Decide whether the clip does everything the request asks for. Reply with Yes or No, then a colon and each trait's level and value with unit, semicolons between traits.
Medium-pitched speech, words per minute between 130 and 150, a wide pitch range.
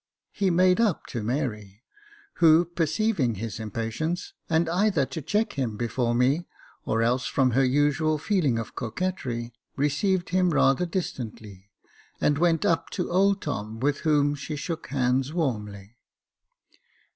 Yes: medium, 145 Hz; average, 140 wpm; wide, 6.4 semitones